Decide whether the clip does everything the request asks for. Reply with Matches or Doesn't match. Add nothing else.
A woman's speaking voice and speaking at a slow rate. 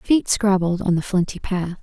Doesn't match